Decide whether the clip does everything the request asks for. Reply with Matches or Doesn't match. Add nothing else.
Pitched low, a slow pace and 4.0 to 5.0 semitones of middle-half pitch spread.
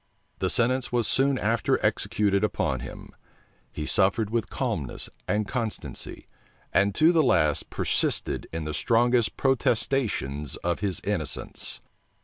Matches